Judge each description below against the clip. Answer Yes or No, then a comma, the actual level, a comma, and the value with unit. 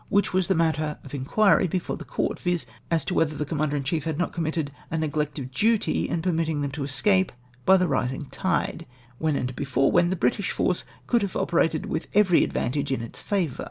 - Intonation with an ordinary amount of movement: Yes, average, 4.1 semitones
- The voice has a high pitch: No, medium, 160 Hz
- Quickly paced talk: Yes, fast, 220 wpm